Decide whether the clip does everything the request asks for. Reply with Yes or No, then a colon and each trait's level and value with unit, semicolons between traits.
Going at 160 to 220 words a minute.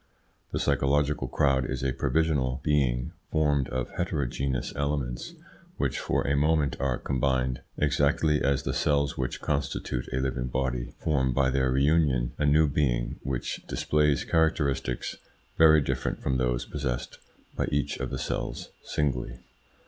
No: average, 140 wpm